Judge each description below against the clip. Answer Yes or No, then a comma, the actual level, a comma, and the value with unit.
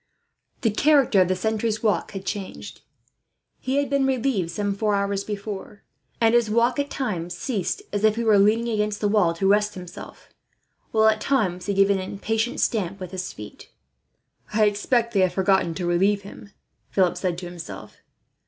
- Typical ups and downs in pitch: Yes, average, 3.0 semitones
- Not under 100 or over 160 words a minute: No, average, 180 wpm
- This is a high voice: Yes, high, 205 Hz